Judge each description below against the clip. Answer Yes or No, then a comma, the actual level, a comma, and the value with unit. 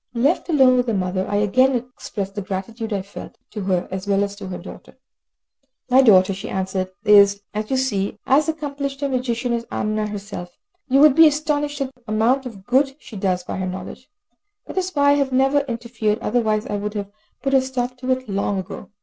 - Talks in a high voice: Yes, high, 230 Hz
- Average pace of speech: No, fast, 215 wpm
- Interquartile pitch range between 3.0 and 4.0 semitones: No, average, 5.0 semitones